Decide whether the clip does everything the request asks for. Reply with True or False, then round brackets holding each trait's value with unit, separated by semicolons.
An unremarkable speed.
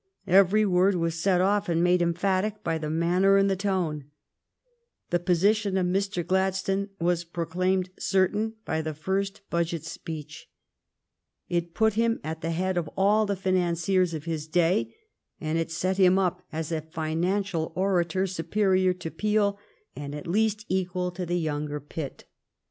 True (160 wpm)